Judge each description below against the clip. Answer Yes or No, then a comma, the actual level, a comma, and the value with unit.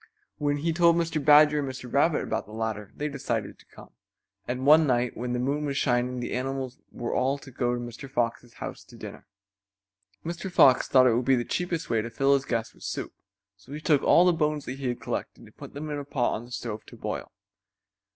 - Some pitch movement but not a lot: Yes, average, 3.4 semitones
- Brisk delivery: Yes, fast, 235 wpm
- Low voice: Yes, low, 130 Hz